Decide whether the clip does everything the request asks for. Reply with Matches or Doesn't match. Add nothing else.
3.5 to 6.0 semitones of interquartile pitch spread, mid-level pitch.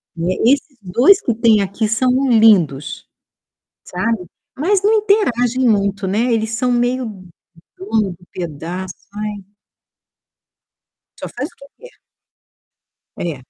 Doesn't match